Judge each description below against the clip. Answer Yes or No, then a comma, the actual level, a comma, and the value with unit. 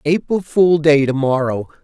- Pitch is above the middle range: No, medium, 150 Hz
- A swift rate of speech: No, slow, 130 wpm